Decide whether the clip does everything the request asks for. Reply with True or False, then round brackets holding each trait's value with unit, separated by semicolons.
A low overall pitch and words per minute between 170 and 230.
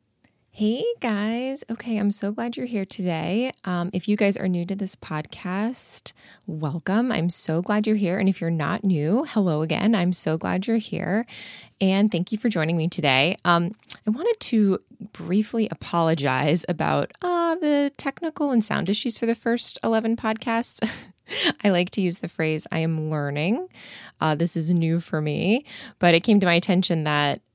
False (195 Hz; 180 wpm)